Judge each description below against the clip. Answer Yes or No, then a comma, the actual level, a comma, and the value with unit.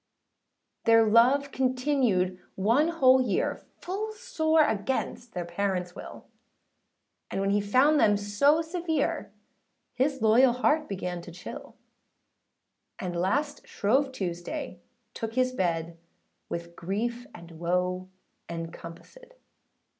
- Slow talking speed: Yes, slow, 110 wpm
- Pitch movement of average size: No, wide, 7.4 semitones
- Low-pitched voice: No, high, 225 Hz